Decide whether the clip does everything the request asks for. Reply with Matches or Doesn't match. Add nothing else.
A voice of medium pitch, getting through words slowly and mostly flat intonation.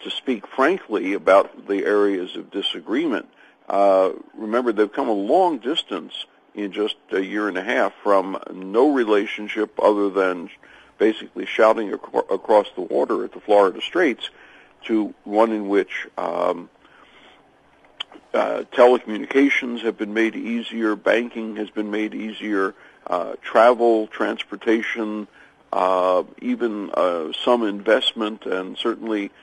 Doesn't match